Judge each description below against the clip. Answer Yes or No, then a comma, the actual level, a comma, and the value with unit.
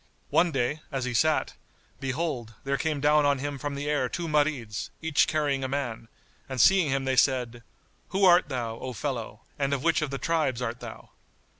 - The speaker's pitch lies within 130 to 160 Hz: Yes, medium, 140 Hz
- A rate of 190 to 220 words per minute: Yes, average, 195 wpm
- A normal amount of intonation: Yes, average, 3.3 semitones